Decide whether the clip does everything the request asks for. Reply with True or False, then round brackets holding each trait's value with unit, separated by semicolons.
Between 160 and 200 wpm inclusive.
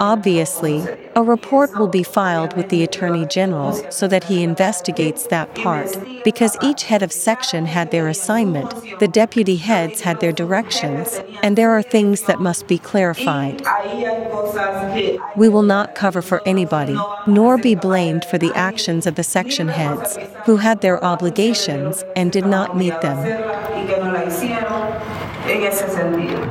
False (145 wpm)